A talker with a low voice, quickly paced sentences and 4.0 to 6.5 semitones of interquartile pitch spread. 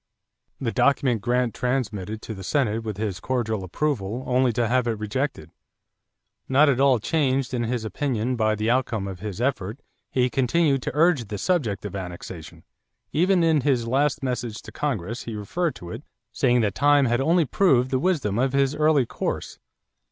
No: low, 125 Hz; average, 180 wpm; average, 4.3 semitones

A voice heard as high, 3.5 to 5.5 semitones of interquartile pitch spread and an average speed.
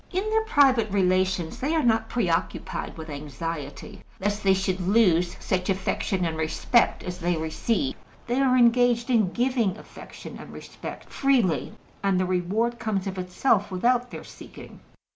Yes: high, 195 Hz; average, 4.9 semitones; average, 160 wpm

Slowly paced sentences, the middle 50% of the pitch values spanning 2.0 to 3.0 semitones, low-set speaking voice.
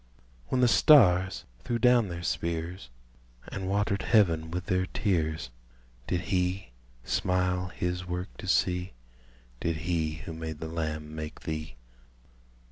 Yes: slow, 130 wpm; average, 2.7 semitones; very low, 90 Hz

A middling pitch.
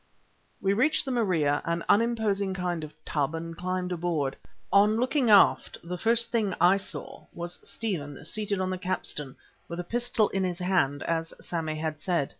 Yes: medium, 180 Hz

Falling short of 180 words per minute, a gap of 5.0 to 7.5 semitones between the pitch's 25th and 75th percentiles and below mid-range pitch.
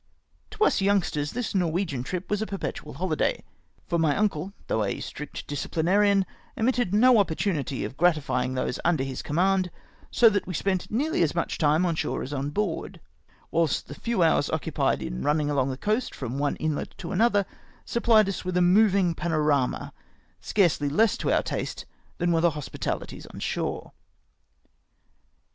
No: average, 170 wpm; average, 5.3 semitones; medium, 175 Hz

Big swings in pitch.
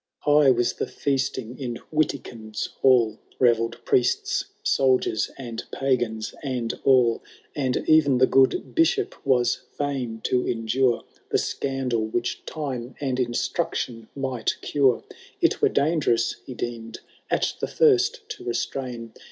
No: average, 2.9 semitones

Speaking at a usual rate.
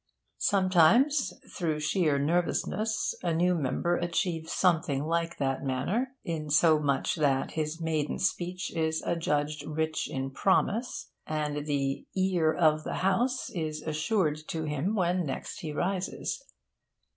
No: slow, 125 wpm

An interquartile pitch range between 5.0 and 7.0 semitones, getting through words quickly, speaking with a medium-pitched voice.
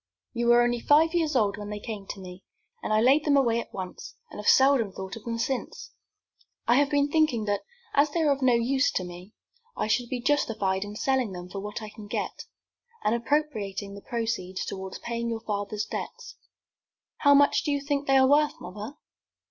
No: wide, 5.4 semitones; fast, 210 wpm; high, 235 Hz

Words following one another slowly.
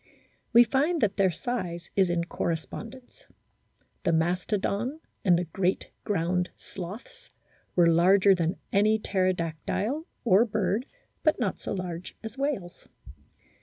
Yes: slow, 125 wpm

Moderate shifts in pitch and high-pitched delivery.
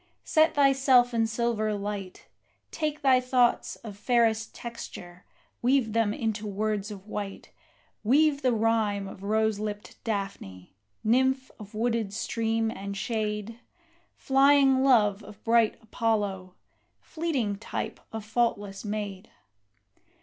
Yes: average, 3.0 semitones; high, 220 Hz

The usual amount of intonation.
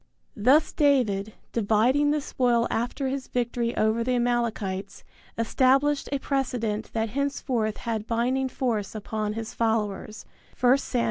Yes: average, 3.3 semitones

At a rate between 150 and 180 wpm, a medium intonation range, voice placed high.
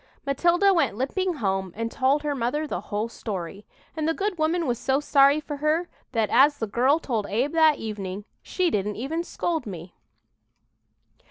No: average, 175 wpm; wide, 6.7 semitones; very high, 275 Hz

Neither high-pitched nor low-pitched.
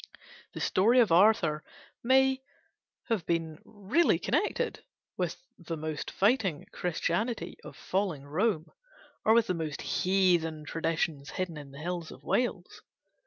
Yes: medium, 180 Hz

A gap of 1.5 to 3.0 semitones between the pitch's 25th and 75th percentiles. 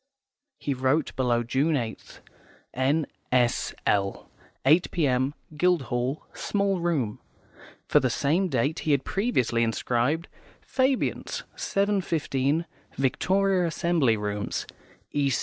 No: wide, 5.5 semitones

